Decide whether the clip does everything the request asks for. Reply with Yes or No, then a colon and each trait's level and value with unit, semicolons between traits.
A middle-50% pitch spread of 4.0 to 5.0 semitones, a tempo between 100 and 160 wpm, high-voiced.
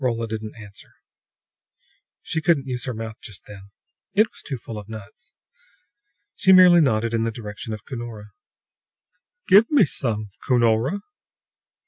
No: average, 4.5 semitones; average, 140 wpm; low, 115 Hz